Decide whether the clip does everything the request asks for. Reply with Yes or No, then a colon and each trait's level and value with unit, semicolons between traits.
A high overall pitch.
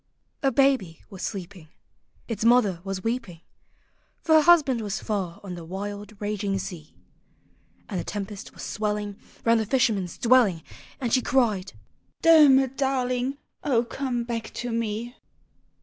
Yes: high, 220 Hz